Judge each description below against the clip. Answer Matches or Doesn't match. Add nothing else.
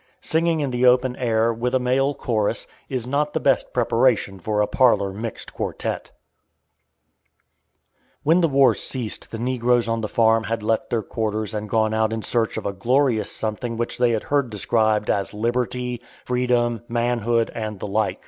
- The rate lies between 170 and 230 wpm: Matches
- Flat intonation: Matches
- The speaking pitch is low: Matches